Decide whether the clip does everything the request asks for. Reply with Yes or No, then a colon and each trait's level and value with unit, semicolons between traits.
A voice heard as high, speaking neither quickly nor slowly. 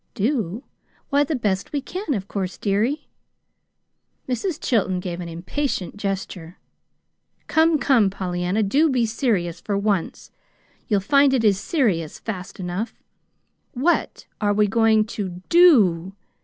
No: high, 210 Hz; slow, 130 wpm